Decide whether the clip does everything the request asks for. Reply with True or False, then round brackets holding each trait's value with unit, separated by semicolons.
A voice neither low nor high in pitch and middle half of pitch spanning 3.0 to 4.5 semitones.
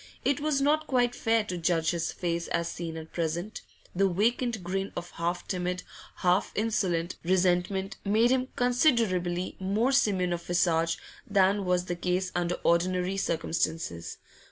True (180 Hz; 3.8 semitones)